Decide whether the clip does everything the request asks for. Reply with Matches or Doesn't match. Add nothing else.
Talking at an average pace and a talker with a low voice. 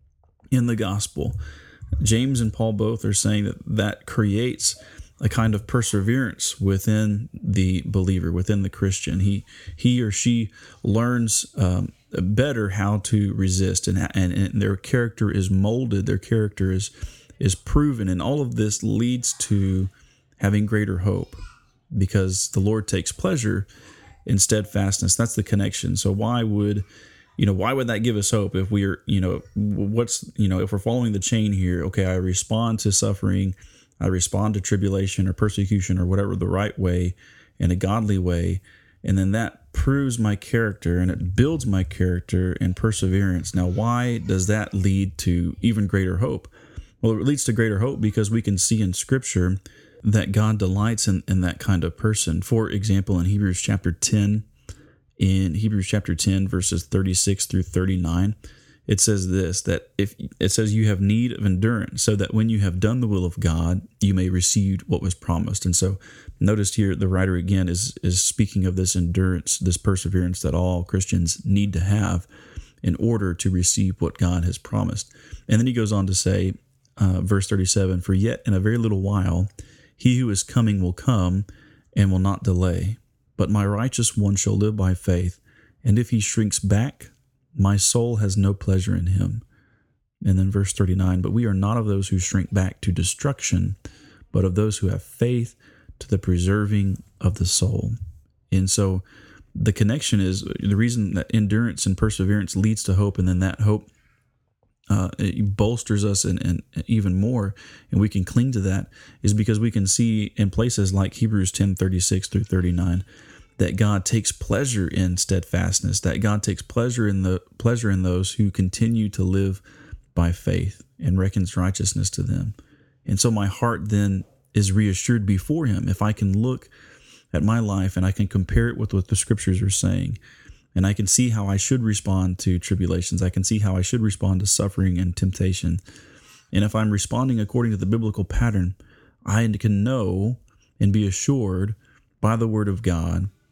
Matches